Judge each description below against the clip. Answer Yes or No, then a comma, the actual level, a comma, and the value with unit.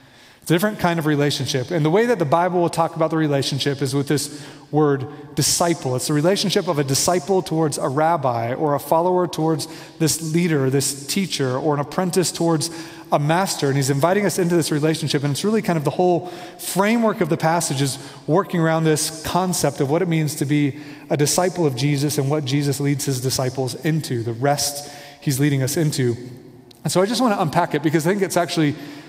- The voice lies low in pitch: No, medium, 155 Hz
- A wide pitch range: No, average, 3.2 semitones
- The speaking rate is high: Yes, fast, 210 wpm